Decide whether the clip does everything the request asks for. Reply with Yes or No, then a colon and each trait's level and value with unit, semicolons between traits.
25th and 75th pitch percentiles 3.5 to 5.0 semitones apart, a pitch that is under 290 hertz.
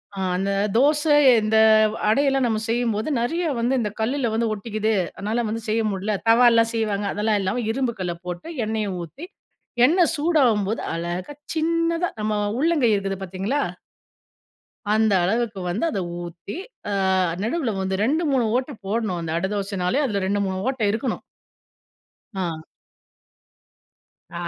Yes: average, 4.5 semitones; high, 220 Hz